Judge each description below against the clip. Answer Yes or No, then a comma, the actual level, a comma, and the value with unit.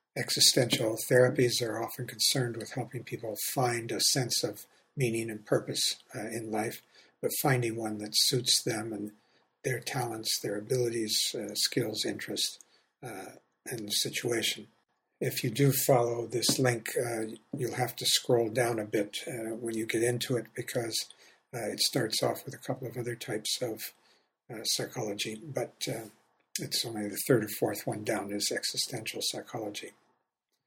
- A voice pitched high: No, low, 120 Hz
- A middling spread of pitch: No, narrow, 1.9 semitones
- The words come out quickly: No, average, 160 wpm